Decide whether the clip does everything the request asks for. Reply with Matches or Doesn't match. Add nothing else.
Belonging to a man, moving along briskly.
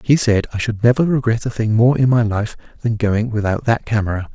Matches